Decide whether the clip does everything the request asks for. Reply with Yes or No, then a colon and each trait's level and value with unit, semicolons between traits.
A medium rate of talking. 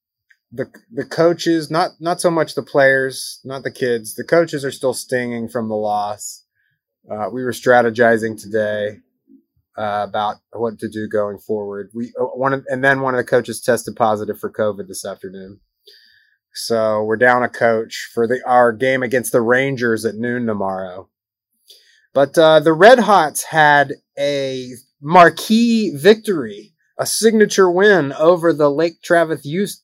Yes: average, 160 wpm